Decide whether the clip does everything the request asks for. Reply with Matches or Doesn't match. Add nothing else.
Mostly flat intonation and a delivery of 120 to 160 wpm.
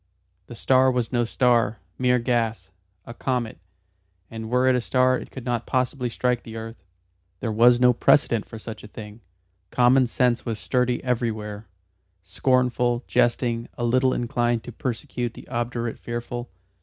Matches